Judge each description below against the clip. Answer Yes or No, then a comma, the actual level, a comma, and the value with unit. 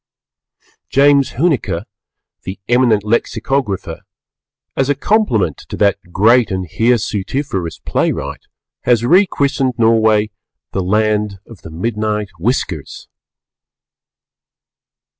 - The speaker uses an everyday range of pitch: Yes, average, 4.4 semitones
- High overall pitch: No, low, 110 Hz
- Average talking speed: No, slow, 95 wpm